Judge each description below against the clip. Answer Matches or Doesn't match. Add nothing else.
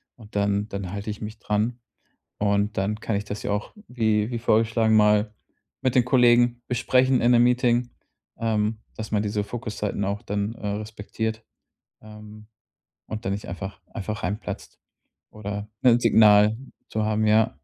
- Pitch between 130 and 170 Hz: Doesn't match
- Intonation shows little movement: Matches